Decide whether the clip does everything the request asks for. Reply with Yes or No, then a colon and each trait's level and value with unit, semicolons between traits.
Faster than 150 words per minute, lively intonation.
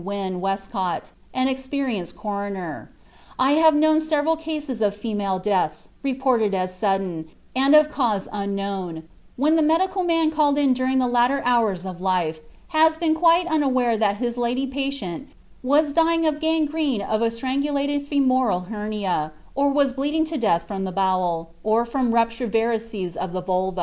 Yes: average, 160 wpm; wide, 6.8 semitones